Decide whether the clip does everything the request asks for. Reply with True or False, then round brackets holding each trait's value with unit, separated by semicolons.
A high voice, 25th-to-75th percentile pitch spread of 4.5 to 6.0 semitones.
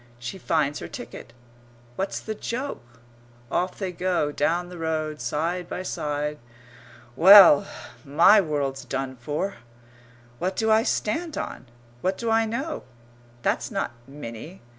False (170 Hz; 5.2 semitones)